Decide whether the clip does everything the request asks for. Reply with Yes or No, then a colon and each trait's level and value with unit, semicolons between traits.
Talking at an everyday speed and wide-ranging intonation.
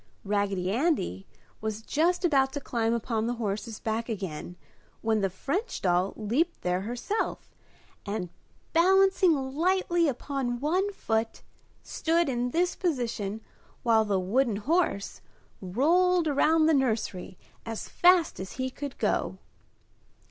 No: slow, 125 wpm; wide, 7.6 semitones